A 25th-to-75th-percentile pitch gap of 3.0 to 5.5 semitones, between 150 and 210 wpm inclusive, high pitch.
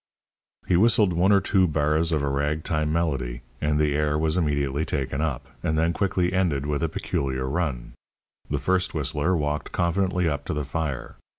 No: average, 3.3 semitones; average, 185 wpm; very low, 75 Hz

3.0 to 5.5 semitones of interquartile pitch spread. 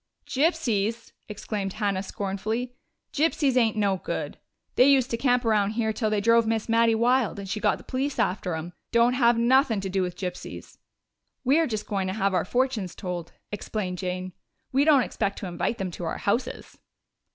Yes: average, 4.2 semitones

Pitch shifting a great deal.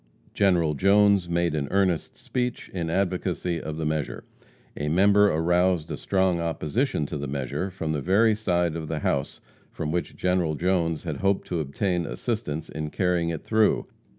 No: average, 3.7 semitones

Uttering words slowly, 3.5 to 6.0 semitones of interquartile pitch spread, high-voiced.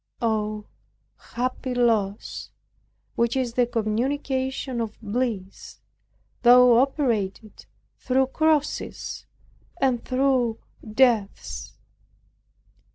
No: slow, 75 wpm; average, 3.1 semitones; high, 245 Hz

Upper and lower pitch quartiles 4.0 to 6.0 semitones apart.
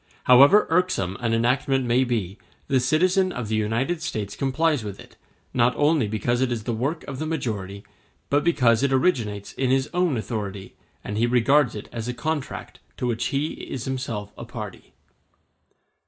Yes: average, 4.6 semitones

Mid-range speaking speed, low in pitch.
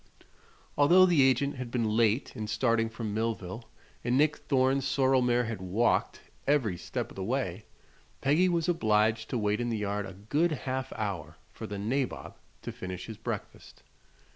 Yes: average, 170 wpm; low, 115 Hz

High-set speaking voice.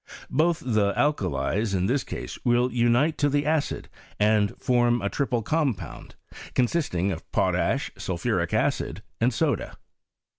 No: low, 120 Hz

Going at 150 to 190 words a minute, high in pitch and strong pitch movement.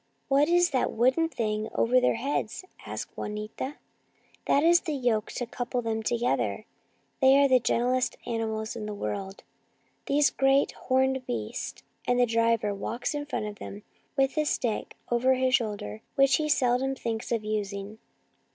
No: average, 170 wpm; high, 245 Hz; average, 3.7 semitones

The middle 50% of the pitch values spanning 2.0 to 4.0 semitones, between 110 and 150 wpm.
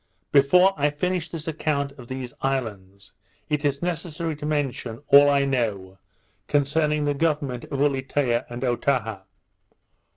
Yes: average, 3.4 semitones; slow, 135 wpm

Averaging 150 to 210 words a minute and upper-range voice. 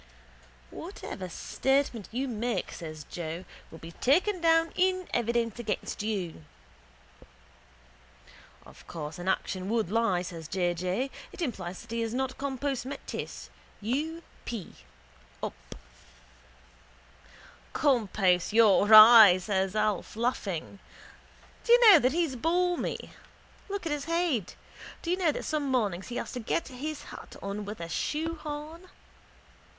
No: slow, 135 wpm; high, 235 Hz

